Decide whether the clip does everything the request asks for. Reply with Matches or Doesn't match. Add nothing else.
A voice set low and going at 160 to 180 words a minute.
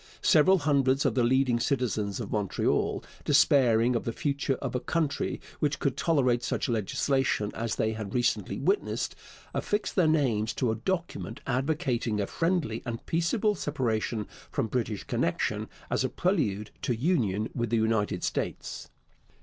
Doesn't match